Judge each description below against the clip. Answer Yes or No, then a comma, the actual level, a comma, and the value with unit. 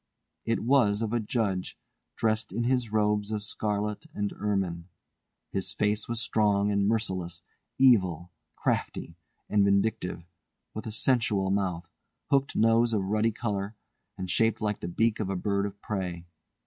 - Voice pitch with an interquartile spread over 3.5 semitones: No, narrow, 2.5 semitones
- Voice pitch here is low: Yes, low, 105 Hz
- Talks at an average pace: Yes, average, 150 wpm